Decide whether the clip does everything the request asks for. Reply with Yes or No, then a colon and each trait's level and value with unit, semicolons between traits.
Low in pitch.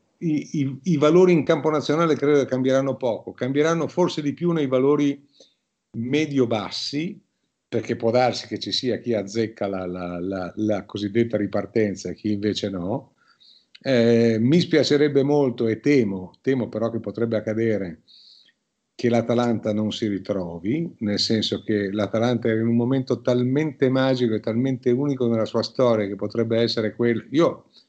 Yes: low, 115 Hz